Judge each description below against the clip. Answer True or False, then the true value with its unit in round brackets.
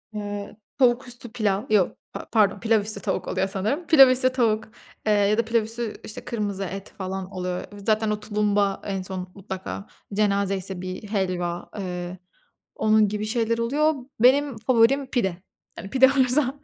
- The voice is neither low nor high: False (210 Hz)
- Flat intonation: False (3.5 semitones)